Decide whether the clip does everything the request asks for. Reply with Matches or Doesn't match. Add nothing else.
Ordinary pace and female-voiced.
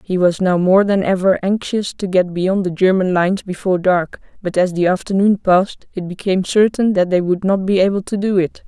Doesn't match